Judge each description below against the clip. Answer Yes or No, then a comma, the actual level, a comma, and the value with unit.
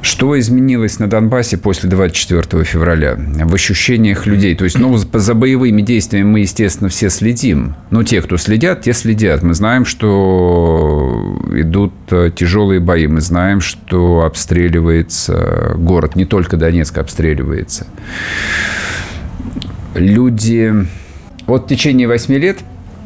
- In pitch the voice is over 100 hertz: No, very low, 95 Hz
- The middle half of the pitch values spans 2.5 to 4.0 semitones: No, average, 4.6 semitones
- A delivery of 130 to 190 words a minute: No, average, 120 wpm